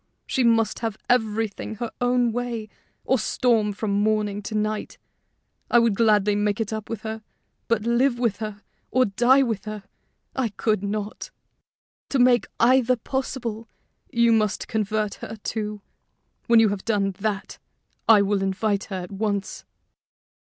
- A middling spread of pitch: No, narrow, 2.2 semitones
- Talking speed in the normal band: Yes, average, 150 wpm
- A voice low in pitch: No, high, 220 Hz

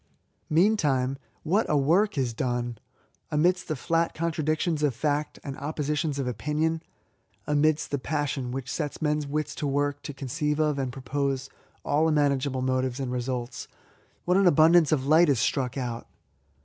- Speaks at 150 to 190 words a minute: Yes, average, 160 wpm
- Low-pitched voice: No, medium, 145 Hz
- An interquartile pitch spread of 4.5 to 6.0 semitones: No, average, 2.8 semitones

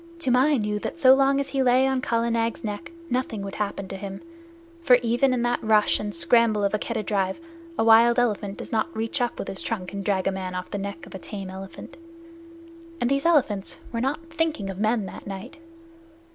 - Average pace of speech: No, fast, 220 wpm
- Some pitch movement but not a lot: Yes, average, 4.3 semitones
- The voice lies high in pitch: Yes, high, 225 Hz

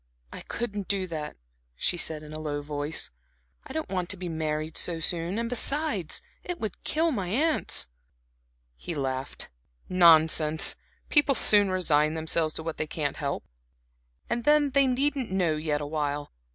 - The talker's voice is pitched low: No, medium, 170 Hz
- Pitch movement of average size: No, wide, 7.0 semitones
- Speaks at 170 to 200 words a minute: No, average, 160 wpm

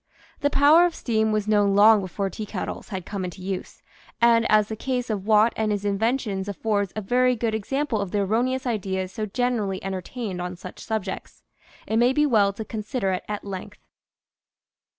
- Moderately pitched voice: No, high, 215 Hz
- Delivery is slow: No, average, 190 wpm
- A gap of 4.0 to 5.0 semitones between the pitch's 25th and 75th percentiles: No, average, 3.2 semitones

